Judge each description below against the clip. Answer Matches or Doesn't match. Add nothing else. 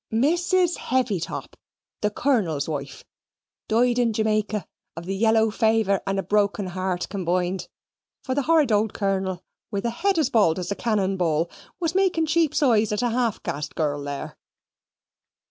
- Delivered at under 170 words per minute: Matches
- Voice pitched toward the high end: Matches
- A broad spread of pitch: Doesn't match